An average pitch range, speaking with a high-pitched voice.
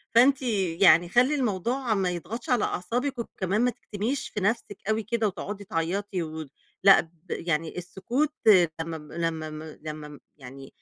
No: wide, 6.2 semitones; high, 195 Hz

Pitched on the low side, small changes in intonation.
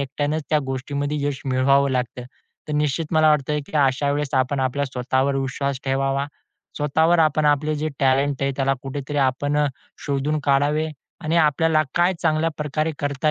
No: medium, 145 Hz; narrow, 2.0 semitones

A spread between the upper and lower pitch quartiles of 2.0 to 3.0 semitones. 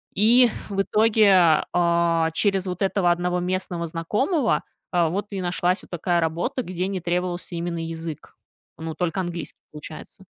Yes: narrow, 2.4 semitones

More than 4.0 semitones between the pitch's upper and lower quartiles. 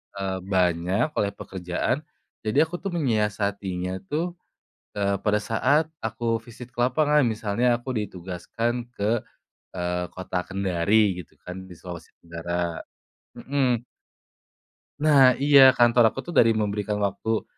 Yes: average, 4.7 semitones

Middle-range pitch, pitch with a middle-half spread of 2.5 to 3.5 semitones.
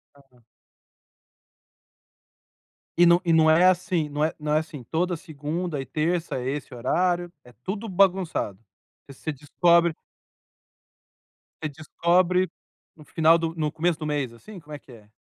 Yes: medium, 160 Hz; average, 3.1 semitones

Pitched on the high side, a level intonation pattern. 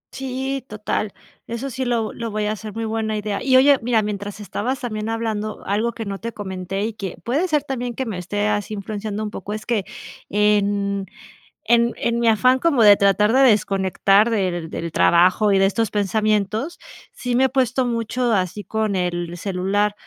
No: high, 215 Hz; average, 3.0 semitones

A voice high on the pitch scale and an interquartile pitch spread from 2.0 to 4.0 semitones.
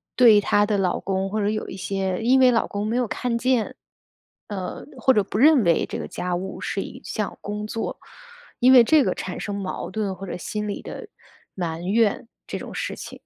Yes: high, 210 Hz; average, 3.3 semitones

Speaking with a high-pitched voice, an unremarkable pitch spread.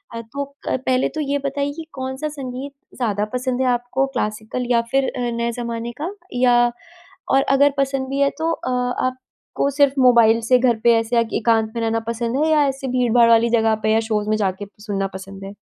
Yes: high, 245 Hz; average, 3.1 semitones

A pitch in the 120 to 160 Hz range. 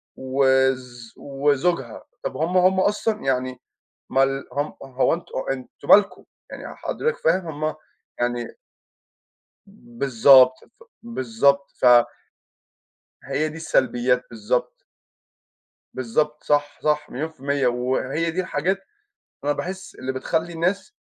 Yes: medium, 140 Hz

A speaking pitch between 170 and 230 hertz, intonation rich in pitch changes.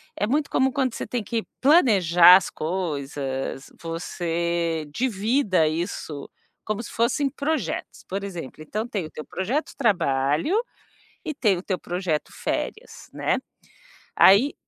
Yes: high, 190 Hz; wide, 6.7 semitones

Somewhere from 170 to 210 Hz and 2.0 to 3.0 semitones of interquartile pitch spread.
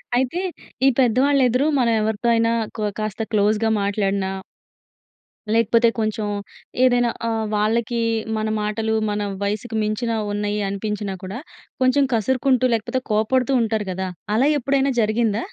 No: high, 225 Hz; narrow, 2.6 semitones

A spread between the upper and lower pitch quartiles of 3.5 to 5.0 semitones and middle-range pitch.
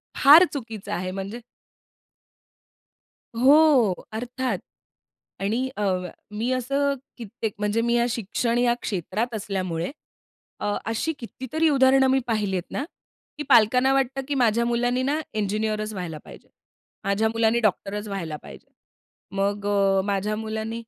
No: average, 3.9 semitones; high, 225 Hz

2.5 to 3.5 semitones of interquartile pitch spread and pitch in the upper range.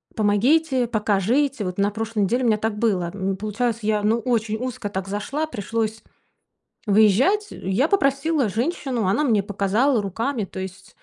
No: average, 3.9 semitones; high, 220 Hz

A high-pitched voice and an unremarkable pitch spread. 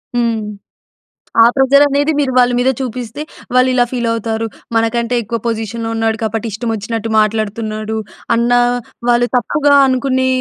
No: high, 235 Hz; narrow, 2.2 semitones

